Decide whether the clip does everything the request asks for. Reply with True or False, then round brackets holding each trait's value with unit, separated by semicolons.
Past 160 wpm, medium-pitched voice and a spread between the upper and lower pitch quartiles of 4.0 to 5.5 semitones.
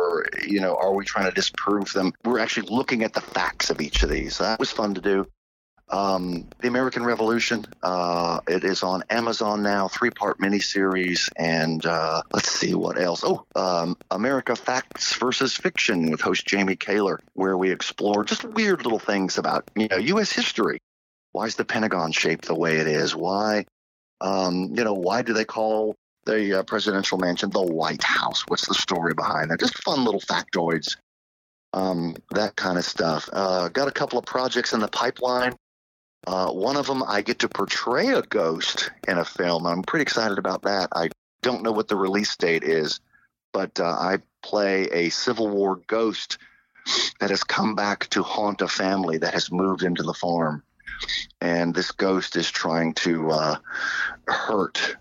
False (180 wpm; 95 Hz; 4.3 semitones)